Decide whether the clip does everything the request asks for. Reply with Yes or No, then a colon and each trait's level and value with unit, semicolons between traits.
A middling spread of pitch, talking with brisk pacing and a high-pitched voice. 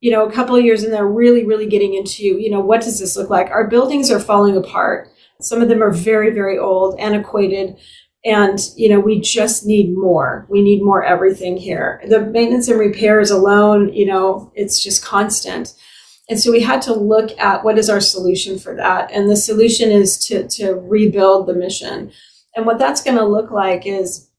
No: narrow, 2.2 semitones; fast, 210 wpm; high, 205 Hz